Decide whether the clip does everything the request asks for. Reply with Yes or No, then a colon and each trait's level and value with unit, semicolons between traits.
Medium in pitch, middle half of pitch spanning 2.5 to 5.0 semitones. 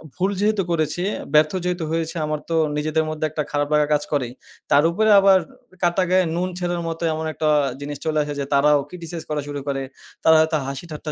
Yes: medium, 160 Hz; average, 2.9 semitones